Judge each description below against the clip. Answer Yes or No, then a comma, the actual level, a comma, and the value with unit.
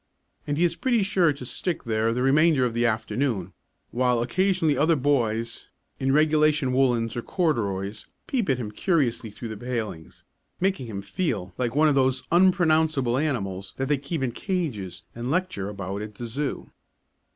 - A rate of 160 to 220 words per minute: Yes, average, 170 wpm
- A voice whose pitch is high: No, low, 130 Hz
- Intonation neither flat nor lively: No, wide, 5.7 semitones